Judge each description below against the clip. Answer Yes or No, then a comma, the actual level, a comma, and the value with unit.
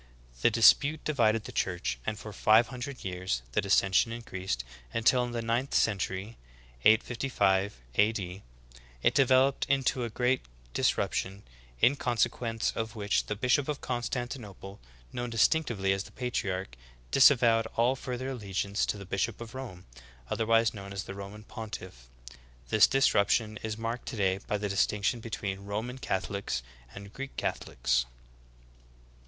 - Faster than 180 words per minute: No, average, 145 wpm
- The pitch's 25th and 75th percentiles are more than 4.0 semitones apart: No, average, 3.7 semitones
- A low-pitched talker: Yes, low, 110 Hz